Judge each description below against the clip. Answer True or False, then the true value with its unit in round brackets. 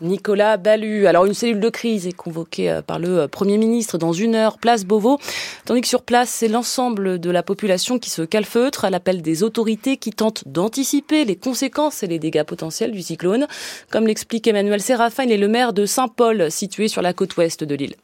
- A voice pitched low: False (215 Hz)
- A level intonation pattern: False (4.2 semitones)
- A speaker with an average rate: True (205 wpm)